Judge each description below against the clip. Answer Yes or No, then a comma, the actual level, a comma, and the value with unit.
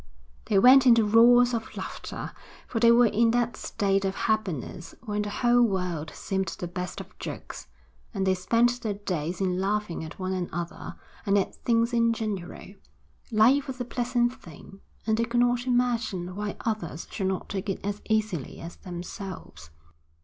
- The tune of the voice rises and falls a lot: No, average, 4.0 semitones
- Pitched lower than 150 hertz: No, high, 210 Hz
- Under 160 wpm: No, average, 170 wpm